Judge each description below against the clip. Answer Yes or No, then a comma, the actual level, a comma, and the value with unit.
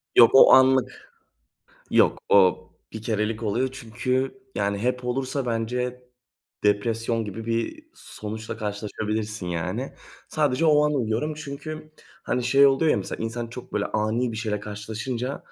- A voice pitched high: No, low, 115 Hz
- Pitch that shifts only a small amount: No, average, 3.4 semitones